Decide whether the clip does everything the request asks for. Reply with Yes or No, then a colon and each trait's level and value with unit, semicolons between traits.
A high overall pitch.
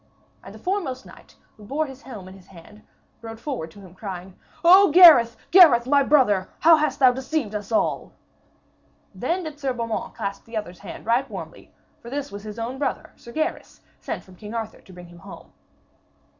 Yes: high, 235 Hz